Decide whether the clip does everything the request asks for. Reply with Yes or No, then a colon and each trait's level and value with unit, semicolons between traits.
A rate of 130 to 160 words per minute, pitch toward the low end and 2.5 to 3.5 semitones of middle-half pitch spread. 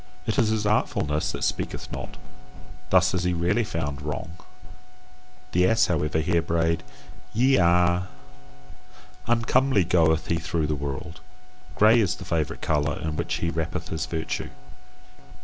Yes: average, 145 wpm; very low, 85 Hz; average, 3.0 semitones